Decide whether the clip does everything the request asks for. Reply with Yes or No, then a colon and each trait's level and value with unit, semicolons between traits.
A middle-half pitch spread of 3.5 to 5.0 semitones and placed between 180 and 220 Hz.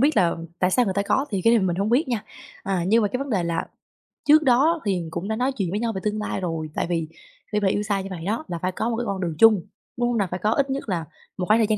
Yes: average, 4.4 semitones; high, 210 Hz